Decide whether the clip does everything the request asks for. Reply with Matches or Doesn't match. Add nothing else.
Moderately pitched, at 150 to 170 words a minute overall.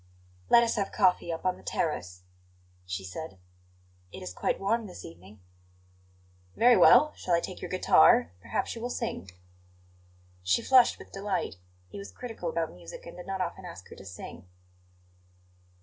Matches